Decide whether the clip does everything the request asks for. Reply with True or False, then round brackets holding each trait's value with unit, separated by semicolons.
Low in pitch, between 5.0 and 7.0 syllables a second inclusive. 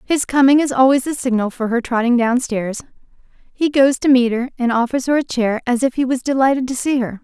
False (255 Hz; 5.7 syllables/s)